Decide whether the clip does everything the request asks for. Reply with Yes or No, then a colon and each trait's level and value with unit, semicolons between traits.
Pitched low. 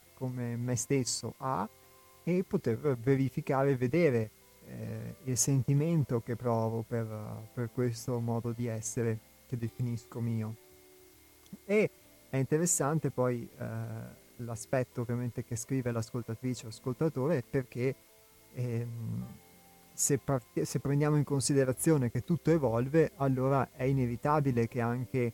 Yes: low, 125 Hz